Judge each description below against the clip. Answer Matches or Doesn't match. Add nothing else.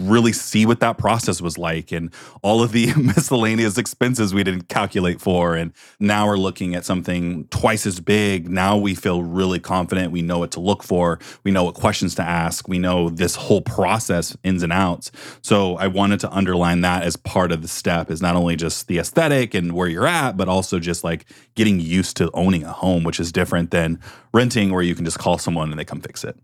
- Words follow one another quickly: Matches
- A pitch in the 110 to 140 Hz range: Doesn't match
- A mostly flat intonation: Doesn't match